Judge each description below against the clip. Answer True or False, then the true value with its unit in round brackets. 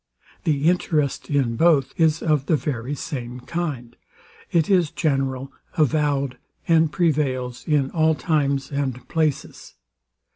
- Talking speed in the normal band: False (120 wpm)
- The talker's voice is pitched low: False (145 Hz)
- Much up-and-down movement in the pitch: False (3.2 semitones)